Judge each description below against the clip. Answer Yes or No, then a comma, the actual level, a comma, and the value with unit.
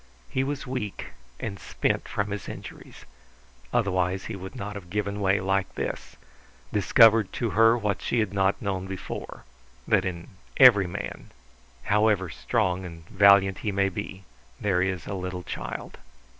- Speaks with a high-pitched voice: No, low, 100 Hz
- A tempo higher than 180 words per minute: No, average, 155 wpm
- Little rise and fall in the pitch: Yes, narrow, 2.1 semitones